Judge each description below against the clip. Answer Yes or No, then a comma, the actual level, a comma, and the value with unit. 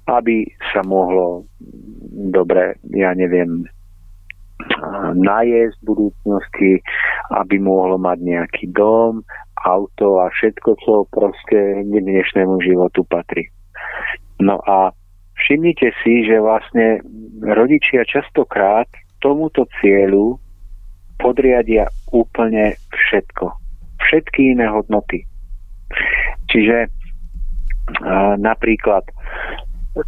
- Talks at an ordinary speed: No, slow, 80 wpm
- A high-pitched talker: No, very low, 95 Hz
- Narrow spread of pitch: No, average, 3.7 semitones